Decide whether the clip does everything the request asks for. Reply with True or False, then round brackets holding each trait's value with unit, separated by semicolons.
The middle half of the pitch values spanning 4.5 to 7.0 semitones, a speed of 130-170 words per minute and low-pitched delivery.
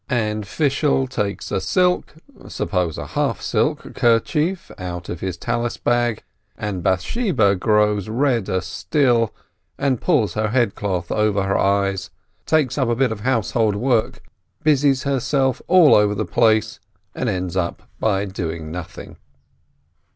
True (5.1 semitones; 140 wpm; 110 Hz)